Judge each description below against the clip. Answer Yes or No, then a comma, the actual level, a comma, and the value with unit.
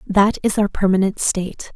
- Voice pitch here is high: Yes, high, 195 Hz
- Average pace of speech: Yes, average, 170 wpm